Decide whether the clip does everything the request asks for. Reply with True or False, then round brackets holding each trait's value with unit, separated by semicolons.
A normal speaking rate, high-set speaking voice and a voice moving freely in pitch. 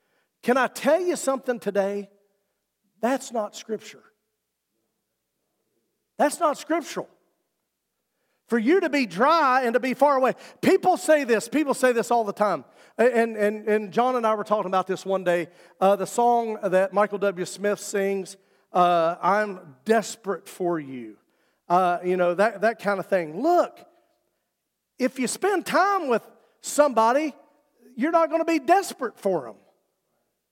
True (155 wpm; 225 Hz; 6.2 semitones)